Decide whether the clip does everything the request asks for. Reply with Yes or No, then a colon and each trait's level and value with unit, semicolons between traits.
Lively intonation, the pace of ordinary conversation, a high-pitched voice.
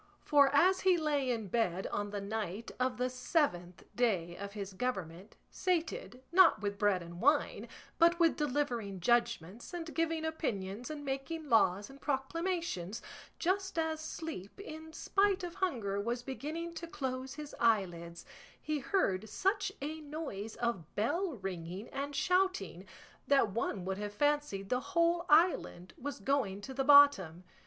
Yes: wide, 8.0 semitones; average, 150 wpm; very high, 260 Hz